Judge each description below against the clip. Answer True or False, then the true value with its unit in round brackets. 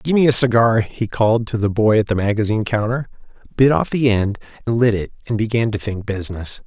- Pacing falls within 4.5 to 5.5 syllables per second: False (5.8 syllables/s)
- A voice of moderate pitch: False (110 Hz)